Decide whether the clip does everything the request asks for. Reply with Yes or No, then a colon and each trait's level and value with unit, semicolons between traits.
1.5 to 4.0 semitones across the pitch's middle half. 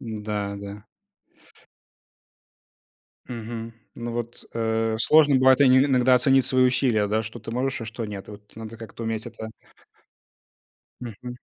Yes: narrow, 2.4 semitones